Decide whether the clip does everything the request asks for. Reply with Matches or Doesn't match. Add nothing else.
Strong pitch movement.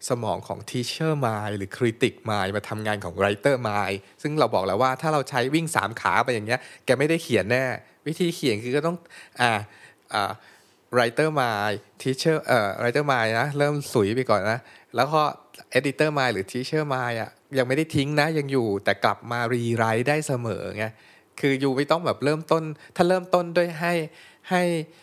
Matches